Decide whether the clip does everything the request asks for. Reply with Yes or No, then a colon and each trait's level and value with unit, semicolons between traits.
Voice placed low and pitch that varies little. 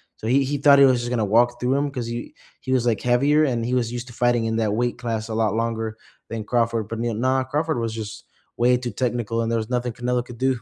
Yes: low, 120 Hz; narrow, 1.8 semitones